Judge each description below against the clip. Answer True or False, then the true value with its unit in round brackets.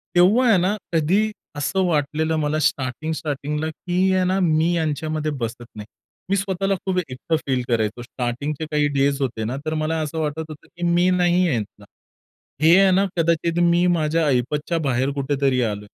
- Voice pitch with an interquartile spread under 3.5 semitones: False (4.1 semitones)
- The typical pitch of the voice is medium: True (155 Hz)